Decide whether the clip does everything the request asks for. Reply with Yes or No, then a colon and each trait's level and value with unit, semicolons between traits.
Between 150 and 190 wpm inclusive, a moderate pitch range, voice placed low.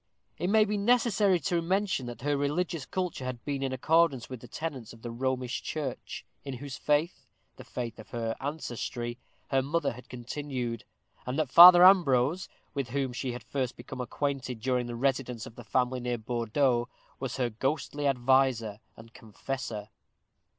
Yes: average, 170 wpm; average, 3.4 semitones; low, 130 Hz